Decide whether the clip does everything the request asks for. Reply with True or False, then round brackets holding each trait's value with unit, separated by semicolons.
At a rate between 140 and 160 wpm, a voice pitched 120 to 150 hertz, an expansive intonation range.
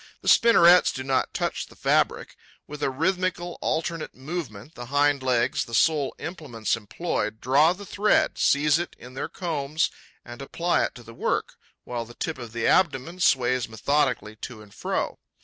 False (170 wpm; 140 Hz; 5.7 semitones)